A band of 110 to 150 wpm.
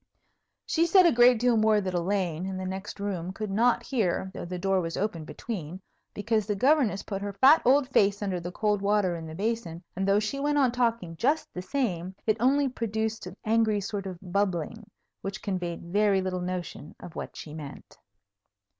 No: average, 200 wpm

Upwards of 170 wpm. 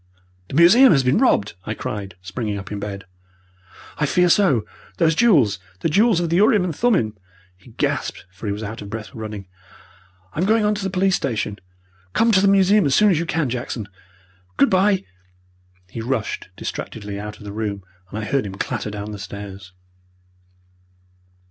Yes: average, 185 wpm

